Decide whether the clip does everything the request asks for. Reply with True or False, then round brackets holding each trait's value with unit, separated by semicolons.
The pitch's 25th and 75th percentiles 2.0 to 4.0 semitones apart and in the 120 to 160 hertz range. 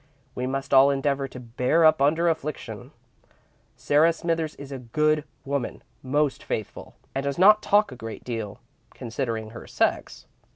True (3.5 semitones; 140 Hz)